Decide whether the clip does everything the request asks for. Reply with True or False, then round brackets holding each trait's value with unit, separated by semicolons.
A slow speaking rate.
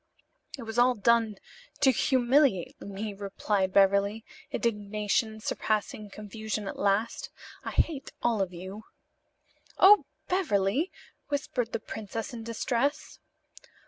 True (110 wpm)